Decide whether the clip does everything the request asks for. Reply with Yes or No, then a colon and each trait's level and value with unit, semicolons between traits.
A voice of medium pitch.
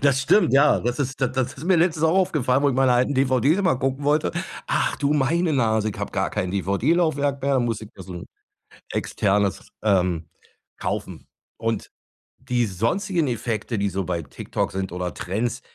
No: low, 125 Hz